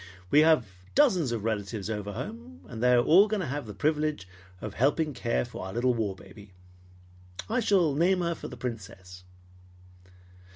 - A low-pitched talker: Yes, low, 125 Hz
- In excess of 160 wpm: Yes, average, 180 wpm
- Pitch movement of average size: No, wide, 6.9 semitones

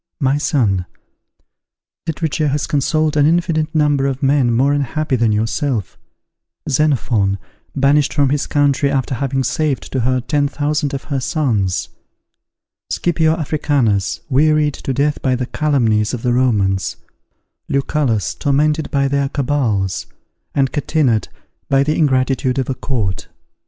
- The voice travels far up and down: No, average, 3.1 semitones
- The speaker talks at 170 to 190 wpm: No, slow, 135 wpm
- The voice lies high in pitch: No, medium, 140 Hz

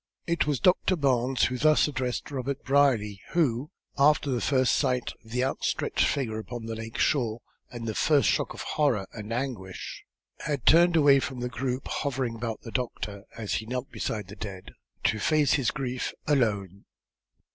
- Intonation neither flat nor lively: Yes, average, 3.9 semitones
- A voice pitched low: Yes, low, 125 Hz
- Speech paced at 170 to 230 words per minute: Yes, average, 175 wpm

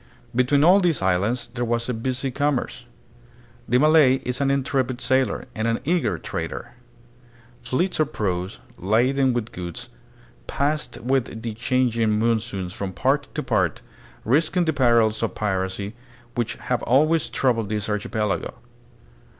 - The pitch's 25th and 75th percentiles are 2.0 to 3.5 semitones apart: No, average, 4.1 semitones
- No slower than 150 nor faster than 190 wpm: No, average, 140 wpm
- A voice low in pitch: Yes, low, 120 Hz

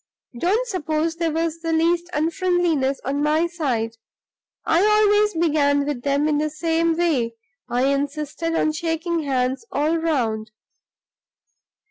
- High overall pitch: Yes, very high, 315 Hz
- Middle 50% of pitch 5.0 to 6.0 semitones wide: No, average, 2.9 semitones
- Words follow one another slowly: Yes, slow, 130 wpm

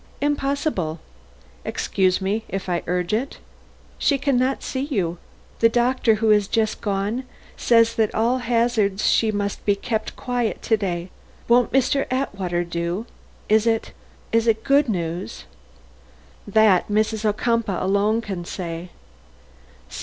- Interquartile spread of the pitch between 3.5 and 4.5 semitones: Yes, average, 3.9 semitones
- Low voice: No, high, 215 Hz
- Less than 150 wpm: Yes, average, 140 wpm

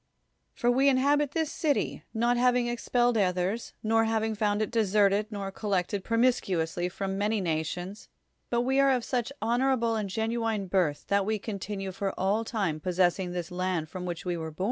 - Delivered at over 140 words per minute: Yes, average, 185 wpm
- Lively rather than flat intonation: No, average, 4.3 semitones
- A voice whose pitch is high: Yes, high, 210 Hz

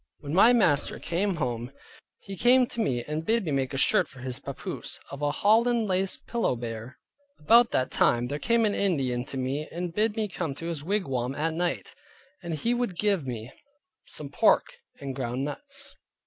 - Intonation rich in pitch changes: Yes, wide, 8.0 semitones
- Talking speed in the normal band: Yes, average, 190 wpm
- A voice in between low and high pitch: Yes, medium, 160 Hz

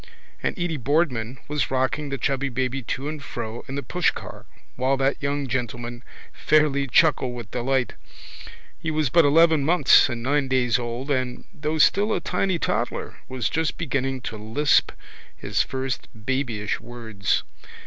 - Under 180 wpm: Yes, average, 155 wpm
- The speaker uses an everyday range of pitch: Yes, average, 3.4 semitones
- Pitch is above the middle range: No, low, 135 Hz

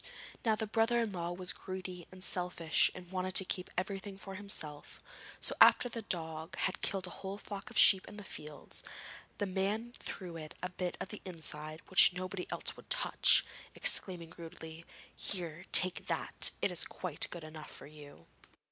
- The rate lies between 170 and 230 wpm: Yes, average, 180 wpm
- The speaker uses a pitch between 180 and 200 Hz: Yes, medium, 185 Hz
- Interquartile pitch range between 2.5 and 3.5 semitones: Yes, average, 3.0 semitones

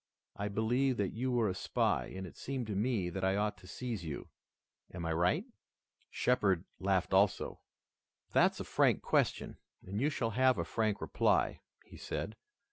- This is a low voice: Yes, low, 105 Hz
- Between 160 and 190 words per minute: Yes, average, 175 wpm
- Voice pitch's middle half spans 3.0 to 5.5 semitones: Yes, average, 4.6 semitones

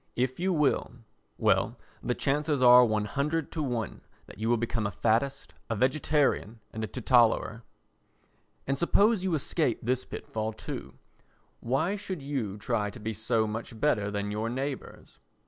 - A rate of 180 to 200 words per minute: No, average, 155 wpm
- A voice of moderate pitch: No, low, 120 Hz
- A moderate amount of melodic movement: Yes, average, 4.8 semitones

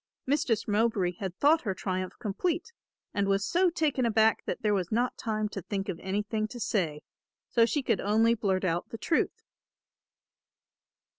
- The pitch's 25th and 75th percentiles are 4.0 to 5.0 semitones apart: No, average, 3.6 semitones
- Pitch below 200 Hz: No, high, 215 Hz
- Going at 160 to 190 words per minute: Yes, average, 165 wpm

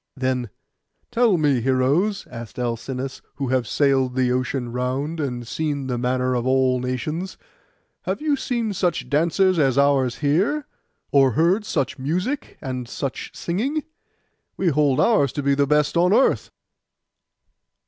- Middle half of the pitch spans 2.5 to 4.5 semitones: No, average, 5.1 semitones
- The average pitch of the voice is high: No, medium, 140 Hz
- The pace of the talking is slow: No, average, 150 wpm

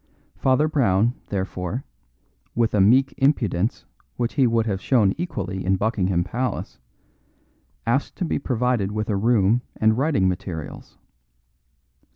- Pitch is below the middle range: Yes, low, 110 Hz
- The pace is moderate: No, slow, 130 wpm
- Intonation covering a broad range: No, average, 4.8 semitones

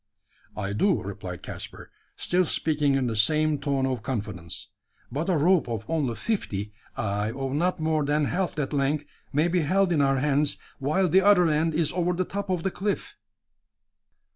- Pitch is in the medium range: Yes, medium, 150 Hz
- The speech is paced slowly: No, average, 180 wpm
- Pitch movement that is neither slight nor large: Yes, average, 4.9 semitones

